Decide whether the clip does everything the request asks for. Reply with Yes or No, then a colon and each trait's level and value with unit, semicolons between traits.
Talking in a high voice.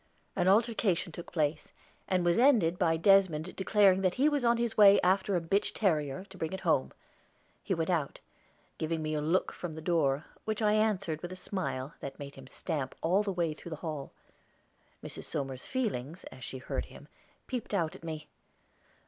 No: medium, 175 Hz